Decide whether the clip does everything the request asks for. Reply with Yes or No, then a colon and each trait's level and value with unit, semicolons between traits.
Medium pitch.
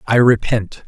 No: low, 110 Hz